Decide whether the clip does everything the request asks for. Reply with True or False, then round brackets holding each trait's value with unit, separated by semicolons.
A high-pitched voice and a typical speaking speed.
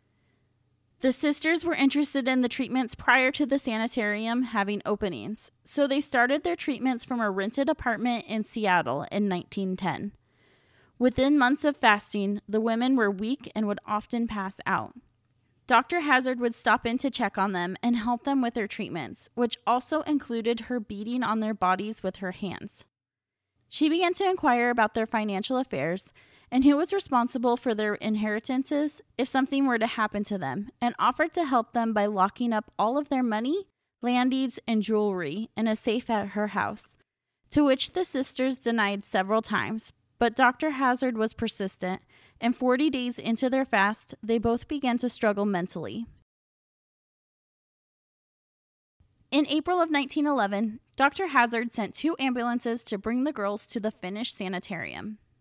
True (235 Hz; 165 wpm)